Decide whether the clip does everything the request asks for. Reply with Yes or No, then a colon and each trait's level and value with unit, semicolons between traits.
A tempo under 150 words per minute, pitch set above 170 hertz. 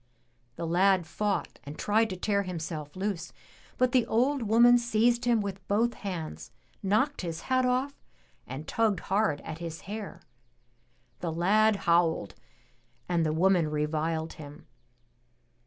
Yes: average, 140 wpm; high, 190 Hz